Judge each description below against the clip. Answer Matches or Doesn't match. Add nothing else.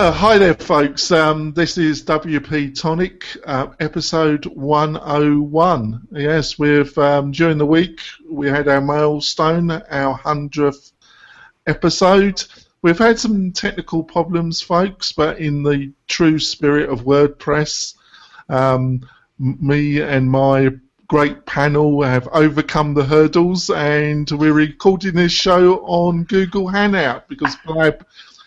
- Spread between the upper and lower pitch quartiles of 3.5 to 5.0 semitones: Doesn't match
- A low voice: Doesn't match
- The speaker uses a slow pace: Matches